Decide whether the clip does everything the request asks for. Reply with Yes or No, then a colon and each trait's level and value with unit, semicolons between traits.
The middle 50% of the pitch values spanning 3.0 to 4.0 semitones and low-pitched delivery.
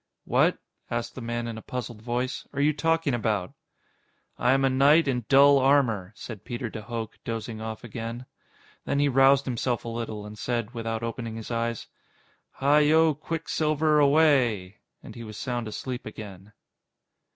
Yes: average, 3.7 semitones; low, 120 Hz